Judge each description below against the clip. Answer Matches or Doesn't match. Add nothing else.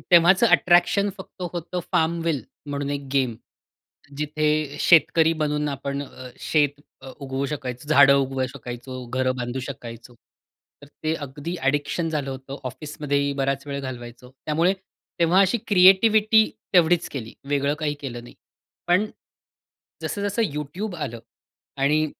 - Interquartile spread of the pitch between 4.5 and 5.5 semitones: Doesn't match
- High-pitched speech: Doesn't match